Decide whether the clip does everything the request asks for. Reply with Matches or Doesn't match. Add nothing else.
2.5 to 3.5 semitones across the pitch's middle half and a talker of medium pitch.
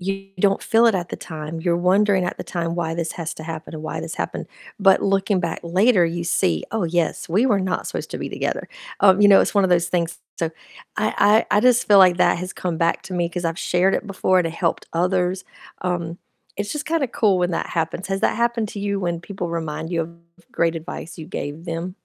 Matches